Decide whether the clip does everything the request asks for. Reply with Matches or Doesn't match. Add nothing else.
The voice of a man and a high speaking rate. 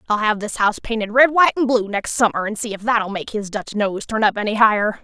Doesn't match